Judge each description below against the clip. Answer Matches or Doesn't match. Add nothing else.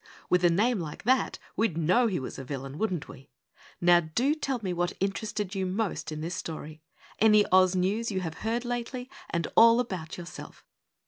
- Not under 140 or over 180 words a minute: Doesn't match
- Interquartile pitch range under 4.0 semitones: Doesn't match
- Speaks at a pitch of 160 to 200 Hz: Matches